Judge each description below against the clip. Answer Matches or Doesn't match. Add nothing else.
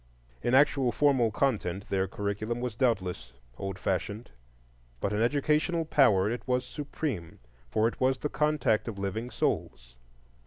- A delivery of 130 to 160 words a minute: Matches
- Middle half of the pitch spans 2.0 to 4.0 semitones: Doesn't match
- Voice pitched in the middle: Doesn't match